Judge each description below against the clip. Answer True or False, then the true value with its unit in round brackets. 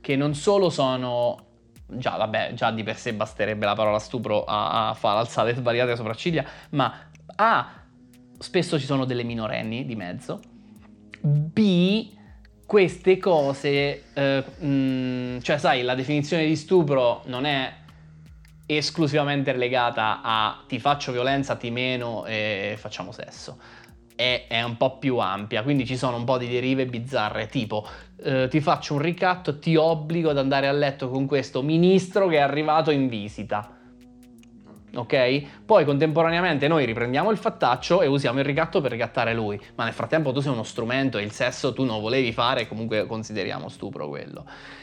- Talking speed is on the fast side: False (160 wpm)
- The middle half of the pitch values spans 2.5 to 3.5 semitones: False (4.1 semitones)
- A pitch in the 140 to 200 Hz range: False (130 Hz)